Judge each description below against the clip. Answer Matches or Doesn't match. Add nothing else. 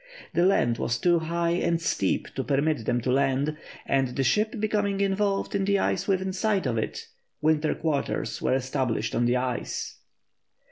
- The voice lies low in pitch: Doesn't match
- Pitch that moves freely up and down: Matches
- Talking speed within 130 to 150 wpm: Doesn't match